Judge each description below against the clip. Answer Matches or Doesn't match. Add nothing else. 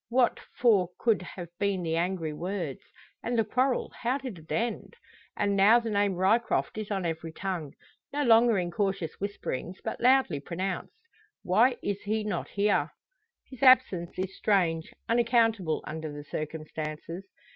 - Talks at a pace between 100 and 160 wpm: Matches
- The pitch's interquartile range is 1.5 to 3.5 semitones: Doesn't match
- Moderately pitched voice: Doesn't match